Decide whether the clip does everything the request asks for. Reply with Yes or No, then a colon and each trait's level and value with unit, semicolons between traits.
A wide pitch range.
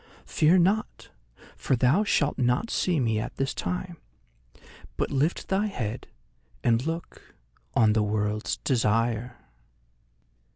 Yes: wide, 7.0 semitones